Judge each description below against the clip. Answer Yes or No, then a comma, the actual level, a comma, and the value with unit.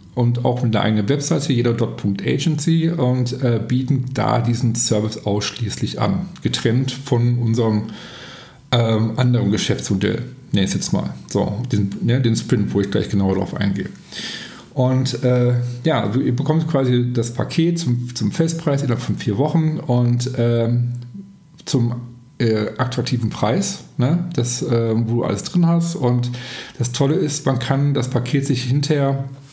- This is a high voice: No, low, 125 Hz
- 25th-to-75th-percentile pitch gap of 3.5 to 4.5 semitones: No, average, 2.8 semitones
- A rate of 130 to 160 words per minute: Yes, average, 150 wpm